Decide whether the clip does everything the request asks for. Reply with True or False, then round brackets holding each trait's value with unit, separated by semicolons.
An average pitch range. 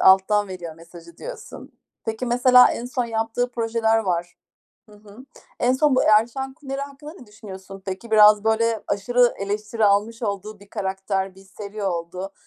True (3.7 semitones)